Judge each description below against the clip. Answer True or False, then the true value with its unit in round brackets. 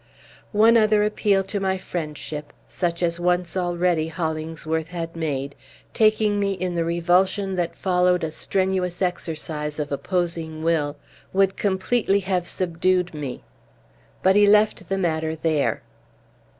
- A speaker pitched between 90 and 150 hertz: False (175 Hz)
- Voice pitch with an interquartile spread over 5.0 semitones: False (3.0 semitones)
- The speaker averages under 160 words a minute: True (135 wpm)